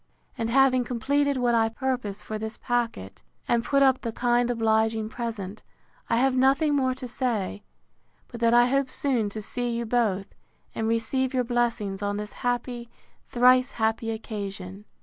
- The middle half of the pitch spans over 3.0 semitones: No, narrow, 2.5 semitones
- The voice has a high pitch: Yes, high, 235 Hz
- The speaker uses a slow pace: No, average, 165 wpm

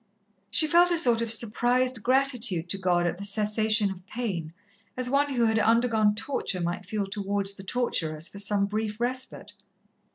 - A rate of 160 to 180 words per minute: Yes, average, 170 wpm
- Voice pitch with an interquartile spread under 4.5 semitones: Yes, average, 3.9 semitones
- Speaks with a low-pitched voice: No, high, 215 Hz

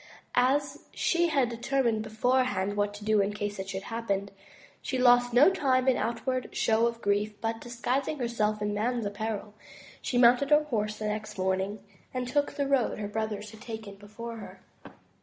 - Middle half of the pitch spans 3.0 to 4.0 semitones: Yes, average, 3.4 semitones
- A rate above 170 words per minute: Yes, average, 180 wpm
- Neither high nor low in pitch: No, high, 225 Hz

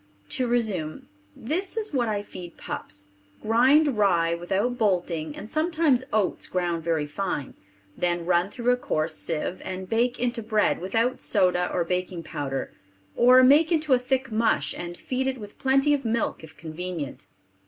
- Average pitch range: No, wide, 6.5 semitones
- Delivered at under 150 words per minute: No, average, 165 wpm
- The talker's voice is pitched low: No, high, 210 Hz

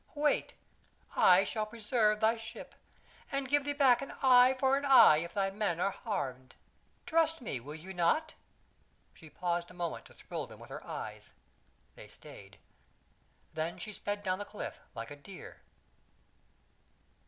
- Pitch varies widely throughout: Yes, wide, 7.0 semitones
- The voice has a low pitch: No, high, 210 Hz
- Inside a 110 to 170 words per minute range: Yes, average, 160 wpm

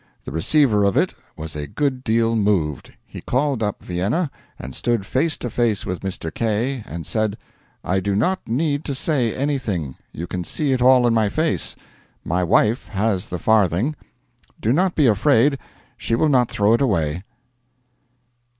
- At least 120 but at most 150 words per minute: No, average, 170 wpm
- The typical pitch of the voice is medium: No, low, 110 Hz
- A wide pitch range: Yes, wide, 5.8 semitones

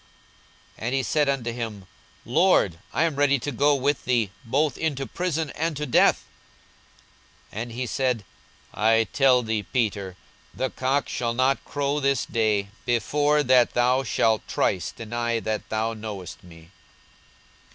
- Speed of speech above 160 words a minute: No, average, 150 wpm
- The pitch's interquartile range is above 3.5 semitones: Yes, average, 4.1 semitones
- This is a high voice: No, low, 125 Hz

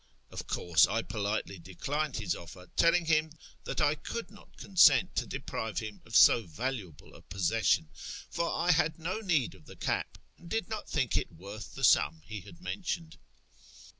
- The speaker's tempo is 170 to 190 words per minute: Yes, average, 175 wpm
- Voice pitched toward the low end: Yes, low, 120 Hz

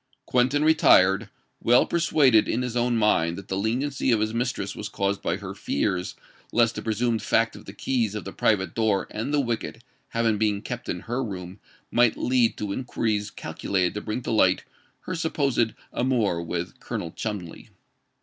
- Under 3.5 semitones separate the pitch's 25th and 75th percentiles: No, average, 3.8 semitones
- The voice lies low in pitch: Yes, low, 110 Hz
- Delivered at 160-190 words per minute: Yes, average, 180 wpm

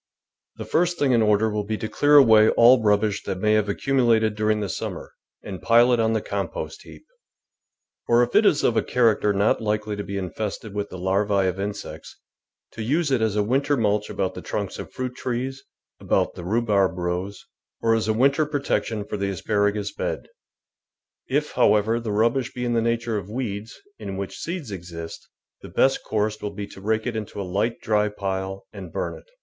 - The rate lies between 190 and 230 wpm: Yes, average, 200 wpm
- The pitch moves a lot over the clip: No, average, 2.7 semitones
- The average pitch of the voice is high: No, low, 110 Hz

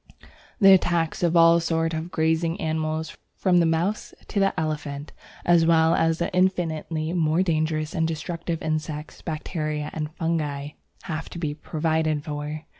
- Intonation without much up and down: Yes, narrow, 1.4 semitones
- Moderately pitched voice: Yes, medium, 160 Hz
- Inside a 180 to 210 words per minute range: No, average, 150 wpm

